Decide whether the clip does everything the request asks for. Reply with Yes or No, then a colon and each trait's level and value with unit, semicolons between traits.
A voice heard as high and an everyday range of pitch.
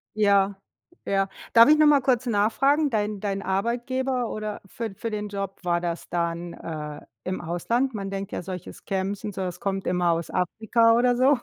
Yes: high, 205 Hz; average, 4.3 semitones